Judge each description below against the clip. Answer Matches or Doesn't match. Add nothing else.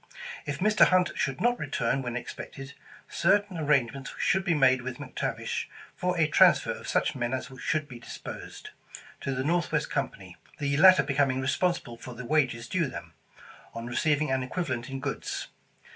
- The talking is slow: Doesn't match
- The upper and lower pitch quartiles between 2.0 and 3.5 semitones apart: Doesn't match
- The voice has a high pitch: Doesn't match